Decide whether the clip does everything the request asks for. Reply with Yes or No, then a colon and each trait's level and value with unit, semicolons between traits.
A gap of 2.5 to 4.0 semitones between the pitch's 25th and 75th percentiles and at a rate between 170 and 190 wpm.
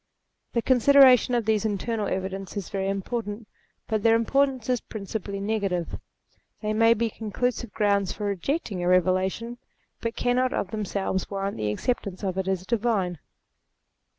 No: average, 3.4 semitones; average, 150 wpm